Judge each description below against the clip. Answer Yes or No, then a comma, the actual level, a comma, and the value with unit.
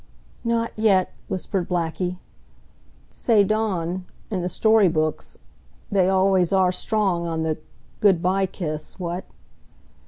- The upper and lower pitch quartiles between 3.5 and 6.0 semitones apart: No, average, 2.7 semitones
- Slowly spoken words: Yes, slow, 120 wpm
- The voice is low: No, medium, 185 Hz